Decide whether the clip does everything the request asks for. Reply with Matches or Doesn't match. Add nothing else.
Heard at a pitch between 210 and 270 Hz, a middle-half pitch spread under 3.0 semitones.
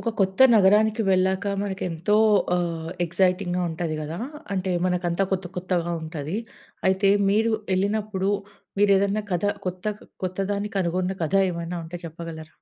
Doesn't match